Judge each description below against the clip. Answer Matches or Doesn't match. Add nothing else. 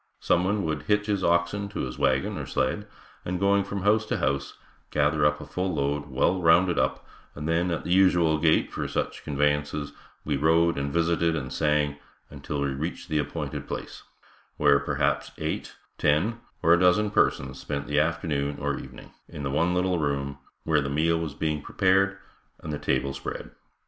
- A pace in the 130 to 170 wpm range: Doesn't match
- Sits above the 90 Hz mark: Doesn't match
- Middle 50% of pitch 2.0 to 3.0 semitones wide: Doesn't match